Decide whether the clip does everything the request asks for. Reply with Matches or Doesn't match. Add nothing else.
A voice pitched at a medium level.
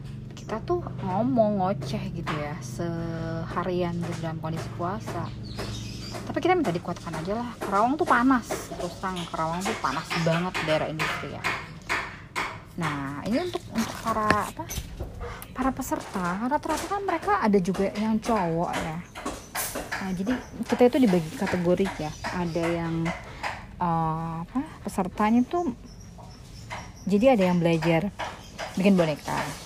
Matches